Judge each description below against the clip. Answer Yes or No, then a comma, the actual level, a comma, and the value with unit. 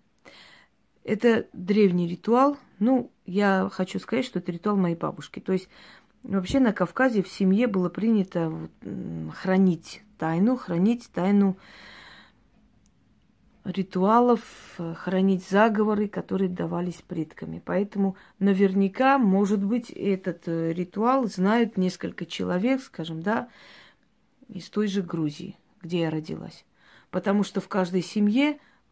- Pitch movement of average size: Yes, average, 3.4 semitones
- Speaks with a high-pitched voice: Yes, high, 195 Hz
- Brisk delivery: No, slow, 110 wpm